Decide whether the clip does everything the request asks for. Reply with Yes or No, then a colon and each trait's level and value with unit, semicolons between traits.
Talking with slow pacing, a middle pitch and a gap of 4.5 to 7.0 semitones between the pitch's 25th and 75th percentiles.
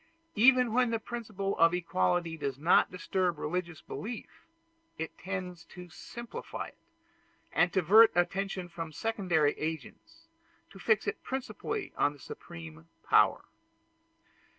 Yes: slow, 130 wpm; medium, 180 Hz; average, 4.9 semitones